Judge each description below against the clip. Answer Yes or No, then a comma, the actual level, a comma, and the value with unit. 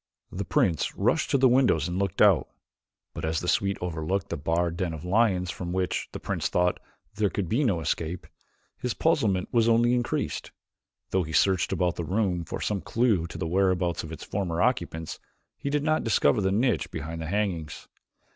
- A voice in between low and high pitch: No, very low, 90 Hz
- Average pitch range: Yes, average, 4.5 semitones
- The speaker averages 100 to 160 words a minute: No, average, 195 wpm